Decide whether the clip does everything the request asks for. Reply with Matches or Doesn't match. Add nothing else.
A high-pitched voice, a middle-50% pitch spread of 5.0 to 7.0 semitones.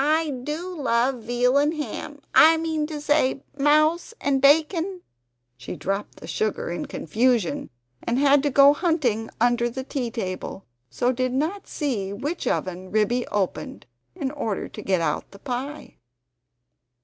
Matches